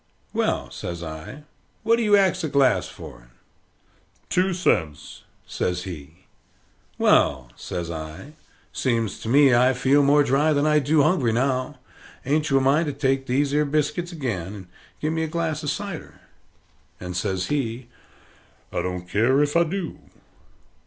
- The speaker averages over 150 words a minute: Yes, average, 160 wpm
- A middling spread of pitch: No, wide, 8.3 semitones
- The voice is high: No, low, 135 Hz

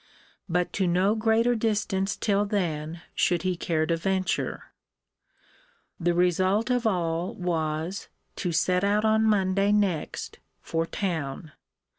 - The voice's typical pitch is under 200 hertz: Yes, medium, 185 Hz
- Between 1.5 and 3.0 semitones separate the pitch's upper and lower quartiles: No, average, 3.6 semitones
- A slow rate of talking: Yes, slow, 125 wpm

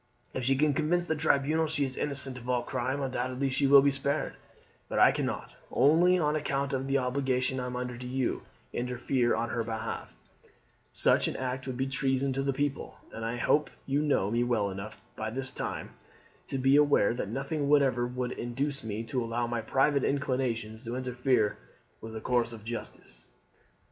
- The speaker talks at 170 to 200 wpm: Yes, average, 195 wpm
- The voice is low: Yes, low, 130 Hz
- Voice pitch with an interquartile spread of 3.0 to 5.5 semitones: No, narrow, 2.5 semitones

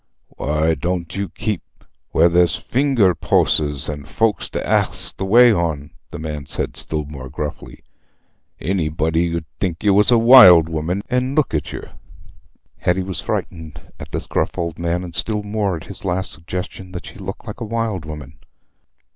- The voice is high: No, very low, 85 Hz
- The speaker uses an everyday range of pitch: Yes, average, 4.5 semitones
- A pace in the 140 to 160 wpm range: No, average, 175 wpm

